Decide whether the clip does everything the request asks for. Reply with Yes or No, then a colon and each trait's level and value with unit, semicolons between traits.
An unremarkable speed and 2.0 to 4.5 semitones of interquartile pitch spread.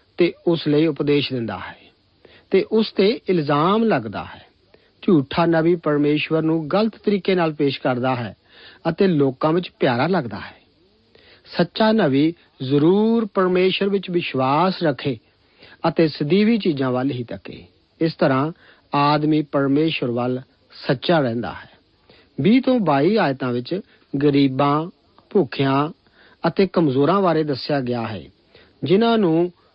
No: average, 130 wpm; average, 5.1 semitones